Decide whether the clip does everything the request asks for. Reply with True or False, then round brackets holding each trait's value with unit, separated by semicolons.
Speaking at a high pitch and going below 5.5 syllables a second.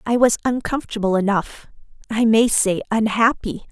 True (220 Hz; 5.1 syllables/s)